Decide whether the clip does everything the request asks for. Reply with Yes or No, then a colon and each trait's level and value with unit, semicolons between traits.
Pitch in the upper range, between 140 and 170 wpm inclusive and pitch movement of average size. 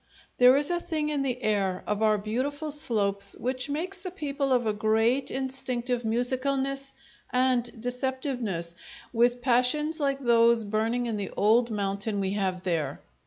Yes: high, 245 Hz; average, 155 wpm; average, 4.1 semitones